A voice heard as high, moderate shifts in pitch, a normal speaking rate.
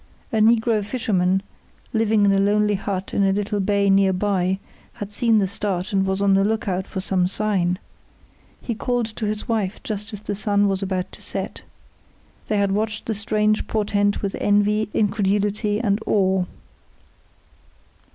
No: high, 205 Hz; narrow, 1.6 semitones; average, 165 wpm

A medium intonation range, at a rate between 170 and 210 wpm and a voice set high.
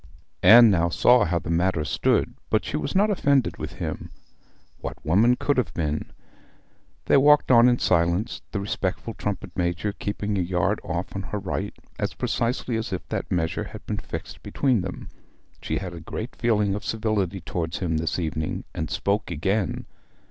No: average, 4.9 semitones; average, 175 wpm; low, 100 Hz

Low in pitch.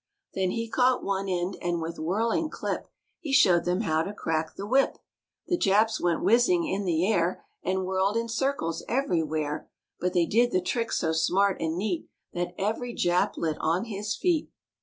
No: high, 190 Hz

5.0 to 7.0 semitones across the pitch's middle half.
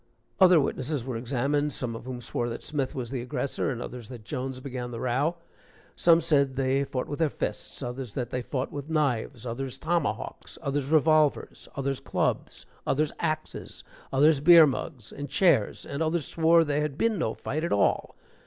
No: average, 3.4 semitones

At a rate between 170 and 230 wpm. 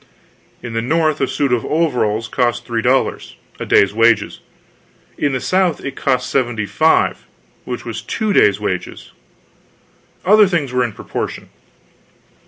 No: average, 145 wpm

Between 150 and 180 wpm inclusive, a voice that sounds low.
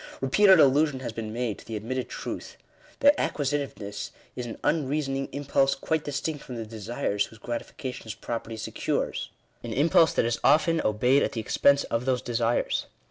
Yes: average, 175 wpm; low, 130 Hz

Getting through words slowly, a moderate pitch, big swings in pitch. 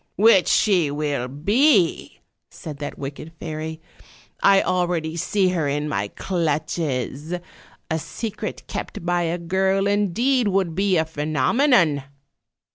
No: slow, 130 wpm; medium, 170 Hz; average, 4.3 semitones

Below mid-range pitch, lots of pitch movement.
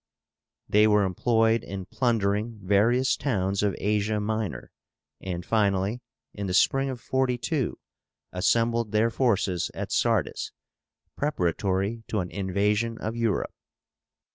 No: low, 105 Hz; average, 3.0 semitones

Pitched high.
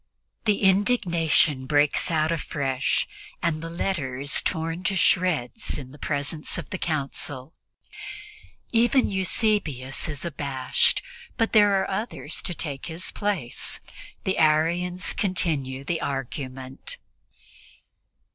No: medium, 160 Hz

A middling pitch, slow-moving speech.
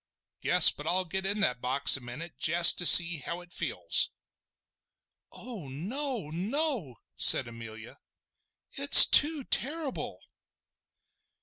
Yes: medium, 175 Hz; slow, 125 wpm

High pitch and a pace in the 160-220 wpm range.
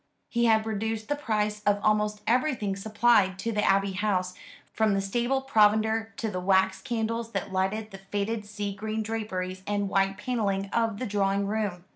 Yes: high, 210 Hz; average, 175 wpm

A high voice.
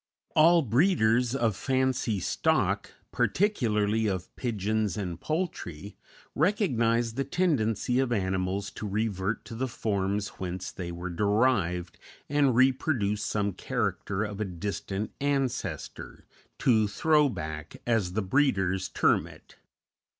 No: low, 110 Hz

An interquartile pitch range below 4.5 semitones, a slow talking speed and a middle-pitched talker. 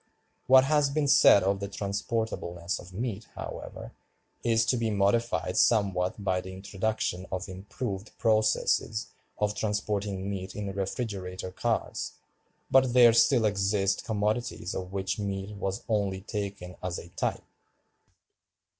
No: average, 2.8 semitones; slow, 130 wpm; low, 100 Hz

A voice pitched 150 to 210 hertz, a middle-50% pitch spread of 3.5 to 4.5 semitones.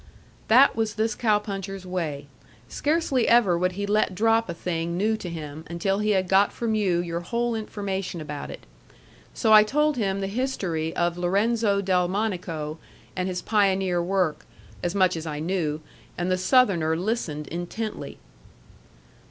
Yes: high, 190 Hz; average, 3.8 semitones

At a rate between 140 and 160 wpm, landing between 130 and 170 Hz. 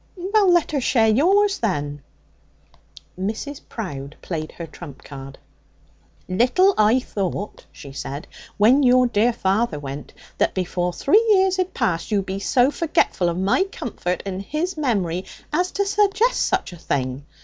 No: average, 150 wpm; high, 215 Hz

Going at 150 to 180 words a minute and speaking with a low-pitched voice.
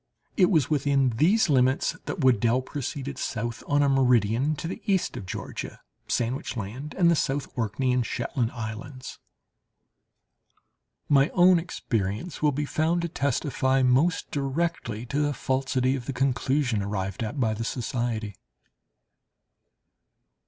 No: average, 140 wpm; low, 130 Hz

